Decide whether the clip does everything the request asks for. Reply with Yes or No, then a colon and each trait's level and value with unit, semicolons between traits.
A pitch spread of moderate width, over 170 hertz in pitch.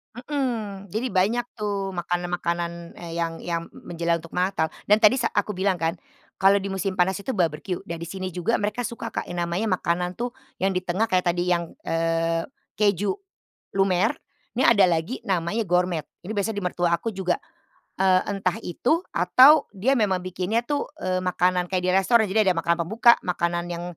Yes: average, 3.3 semitones; medium, 185 Hz